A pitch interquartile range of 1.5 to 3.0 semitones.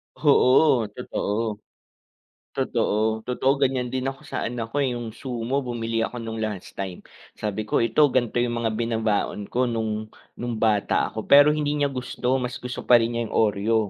Yes: narrow, 2.5 semitones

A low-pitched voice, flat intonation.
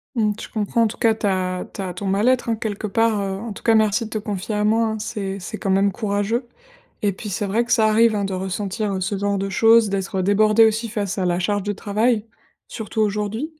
No: high, 210 Hz; narrow, 2.2 semitones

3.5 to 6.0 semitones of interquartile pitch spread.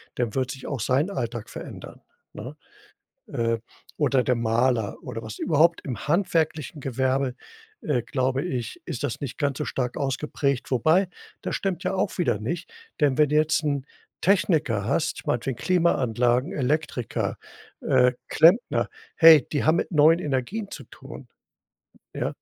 Yes: average, 4.4 semitones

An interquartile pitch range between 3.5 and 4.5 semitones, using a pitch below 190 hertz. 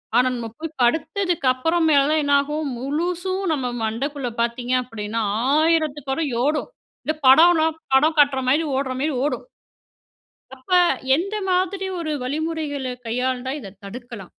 No: average, 4.2 semitones; very high, 285 Hz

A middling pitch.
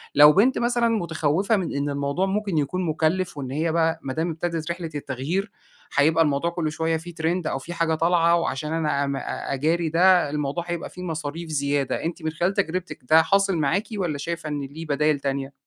Yes: medium, 160 Hz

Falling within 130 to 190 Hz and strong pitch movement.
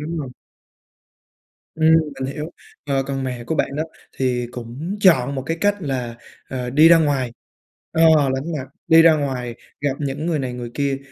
No: medium, 140 Hz; average, 3.9 semitones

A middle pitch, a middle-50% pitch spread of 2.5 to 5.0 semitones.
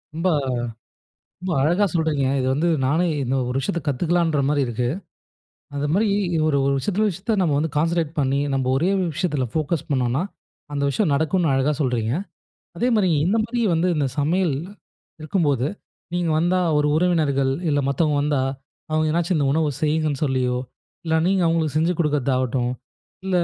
Yes: medium, 155 Hz; average, 3.9 semitones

